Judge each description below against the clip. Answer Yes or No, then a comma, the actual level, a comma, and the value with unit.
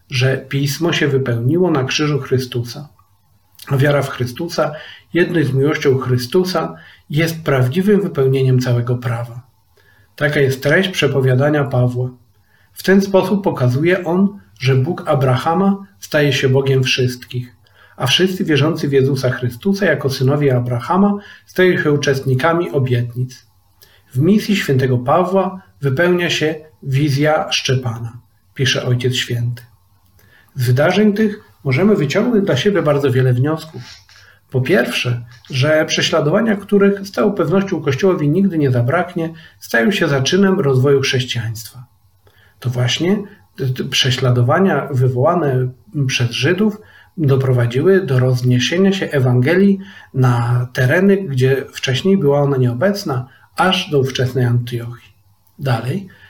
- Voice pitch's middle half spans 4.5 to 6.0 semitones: Yes, average, 5.3 semitones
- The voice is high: No, low, 135 Hz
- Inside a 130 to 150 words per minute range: No, average, 120 wpm